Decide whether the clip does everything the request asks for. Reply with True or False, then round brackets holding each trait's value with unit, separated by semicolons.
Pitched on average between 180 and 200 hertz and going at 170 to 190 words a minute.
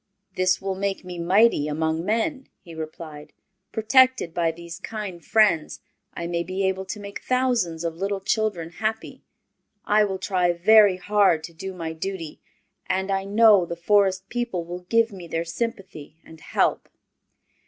False (190 Hz; 160 wpm)